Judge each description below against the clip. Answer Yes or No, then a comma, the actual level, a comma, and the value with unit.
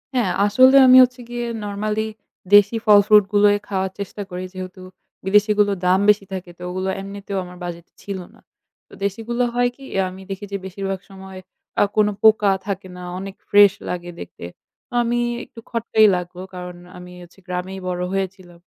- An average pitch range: No, narrow, 2.2 semitones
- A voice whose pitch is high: Yes, high, 195 Hz